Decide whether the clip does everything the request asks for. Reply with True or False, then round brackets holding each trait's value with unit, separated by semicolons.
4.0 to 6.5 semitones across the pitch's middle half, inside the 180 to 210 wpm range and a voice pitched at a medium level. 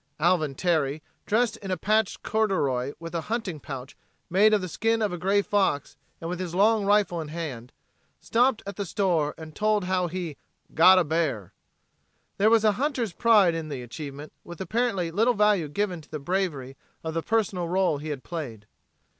True (5.1 semitones; 190 wpm; 180 Hz)